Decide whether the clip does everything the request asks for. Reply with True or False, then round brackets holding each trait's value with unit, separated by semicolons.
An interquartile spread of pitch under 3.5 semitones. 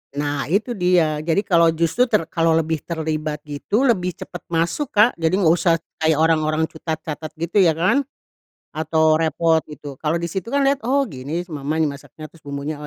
True (2.5 semitones)